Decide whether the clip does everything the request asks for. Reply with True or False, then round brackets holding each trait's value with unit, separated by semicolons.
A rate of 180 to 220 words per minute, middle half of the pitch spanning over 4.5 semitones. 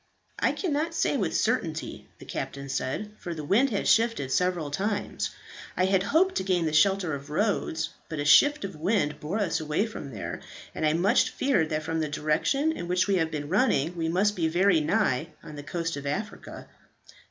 True (200 wpm; 5.1 semitones)